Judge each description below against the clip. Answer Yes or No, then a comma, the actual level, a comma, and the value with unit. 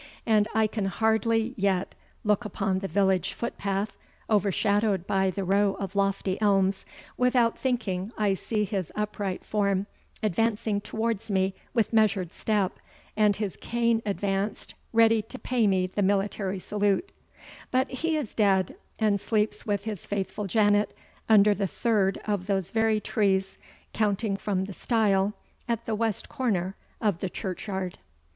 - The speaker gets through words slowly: No, average, 145 wpm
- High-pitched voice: Yes, high, 205 Hz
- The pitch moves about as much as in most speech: No, narrow, 2.2 semitones